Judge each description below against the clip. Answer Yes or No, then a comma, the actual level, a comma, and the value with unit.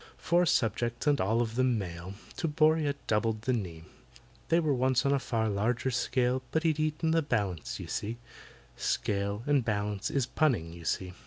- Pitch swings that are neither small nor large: No, wide, 5.9 semitones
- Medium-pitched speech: No, low, 120 Hz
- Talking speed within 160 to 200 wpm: Yes, average, 180 wpm